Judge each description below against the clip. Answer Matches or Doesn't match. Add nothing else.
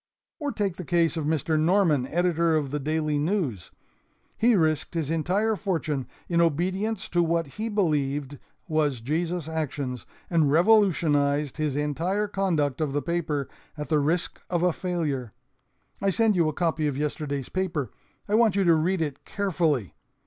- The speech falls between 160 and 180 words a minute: Matches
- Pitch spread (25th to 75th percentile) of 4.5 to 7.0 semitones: Doesn't match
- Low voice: Doesn't match